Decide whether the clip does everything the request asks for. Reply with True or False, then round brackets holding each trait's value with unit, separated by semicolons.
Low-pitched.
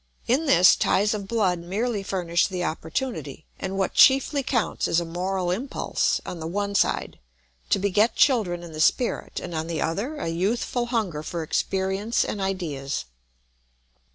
False (190 Hz)